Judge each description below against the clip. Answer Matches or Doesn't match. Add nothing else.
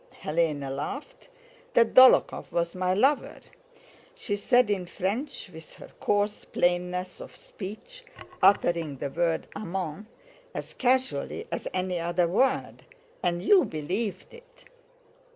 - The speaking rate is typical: Doesn't match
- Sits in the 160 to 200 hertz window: Matches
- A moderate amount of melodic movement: Doesn't match